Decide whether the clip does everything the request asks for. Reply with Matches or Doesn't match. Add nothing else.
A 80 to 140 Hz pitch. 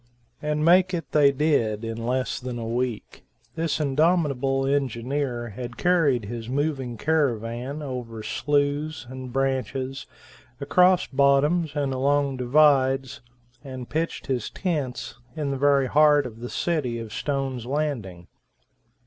Matches